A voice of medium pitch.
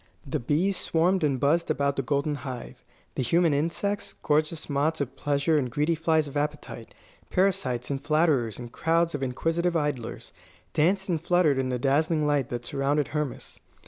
Yes: medium, 150 Hz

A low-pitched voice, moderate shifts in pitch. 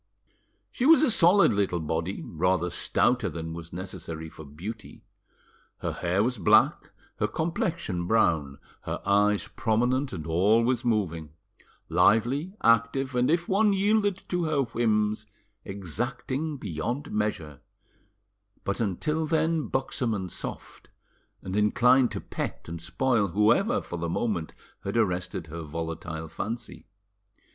No: low, 105 Hz; wide, 7.3 semitones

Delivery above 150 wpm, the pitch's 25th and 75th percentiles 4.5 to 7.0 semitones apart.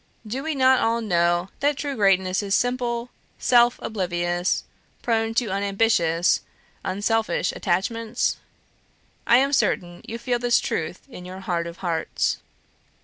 No: slow, 135 wpm; average, 5.1 semitones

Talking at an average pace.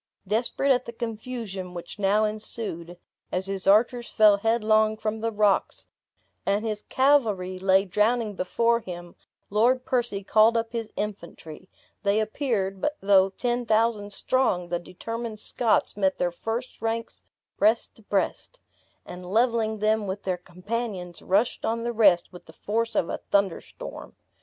Yes: average, 150 wpm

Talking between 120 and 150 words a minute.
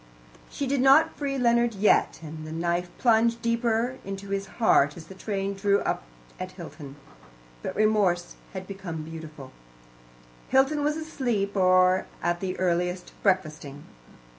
Yes: average, 140 wpm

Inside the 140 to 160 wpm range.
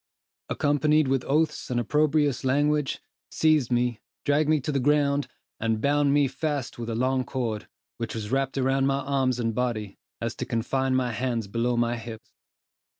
No: average, 175 wpm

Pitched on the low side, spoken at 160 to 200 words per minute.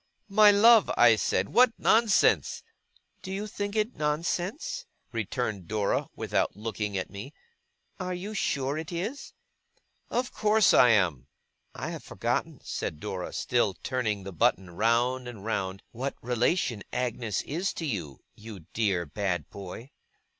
No: low, 120 Hz; average, 145 wpm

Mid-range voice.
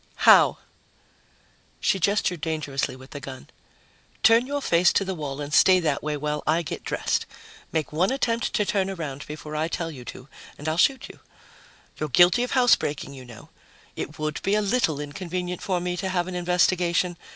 Yes: medium, 170 Hz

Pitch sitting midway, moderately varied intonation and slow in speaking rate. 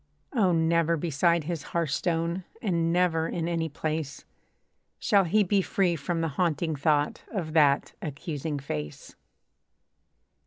No: medium, 165 Hz; narrow, 2.3 semitones; slow, 125 wpm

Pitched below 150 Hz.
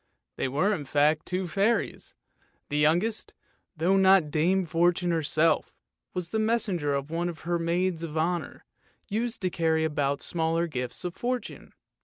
No: medium, 170 Hz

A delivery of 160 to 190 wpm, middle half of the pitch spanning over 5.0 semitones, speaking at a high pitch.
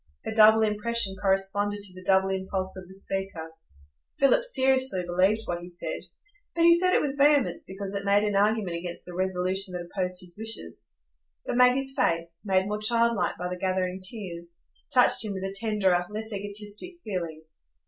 No: average, 180 wpm; average, 3.1 semitones; high, 195 Hz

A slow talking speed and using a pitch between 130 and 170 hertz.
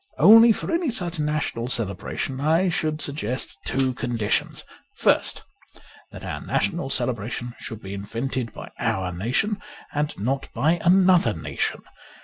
Yes: slow, 130 wpm; low, 135 Hz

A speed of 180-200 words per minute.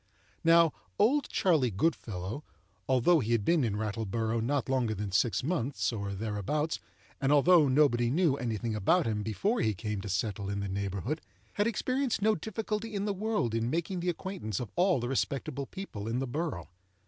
Yes: average, 185 wpm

